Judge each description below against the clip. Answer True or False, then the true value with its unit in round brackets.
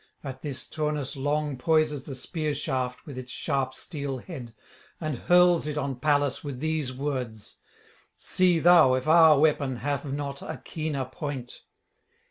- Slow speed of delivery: False (150 wpm)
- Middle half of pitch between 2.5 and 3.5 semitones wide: True (2.9 semitones)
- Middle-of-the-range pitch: True (145 Hz)